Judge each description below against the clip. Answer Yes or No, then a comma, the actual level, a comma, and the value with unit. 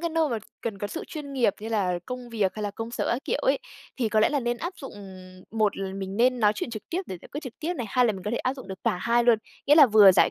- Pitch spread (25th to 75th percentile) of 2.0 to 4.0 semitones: No, average, 4.6 semitones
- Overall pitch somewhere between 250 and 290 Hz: No, high, 235 Hz